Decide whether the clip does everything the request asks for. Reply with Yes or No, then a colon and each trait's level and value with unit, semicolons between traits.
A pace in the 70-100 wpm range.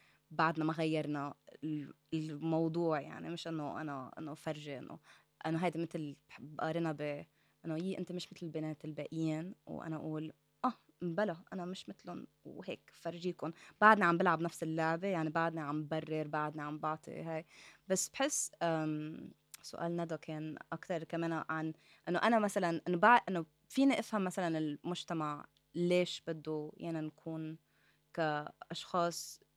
No: fast, 135 wpm